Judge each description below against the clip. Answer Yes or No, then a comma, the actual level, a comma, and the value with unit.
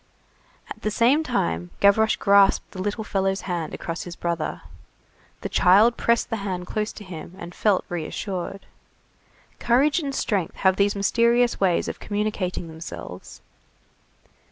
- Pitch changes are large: No, average, 3.8 semitones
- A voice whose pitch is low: No, high, 195 Hz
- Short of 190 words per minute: Yes, average, 140 wpm